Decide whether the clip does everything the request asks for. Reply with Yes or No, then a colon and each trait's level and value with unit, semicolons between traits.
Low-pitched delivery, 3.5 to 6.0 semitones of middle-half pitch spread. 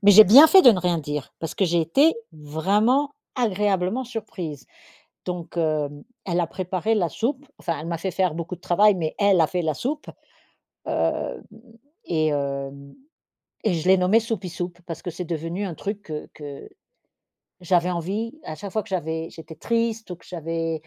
No: medium, 180 Hz; average, 4.3 semitones